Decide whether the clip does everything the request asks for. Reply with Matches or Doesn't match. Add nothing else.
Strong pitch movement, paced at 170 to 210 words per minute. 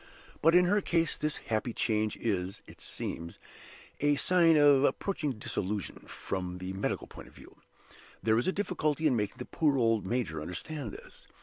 Matches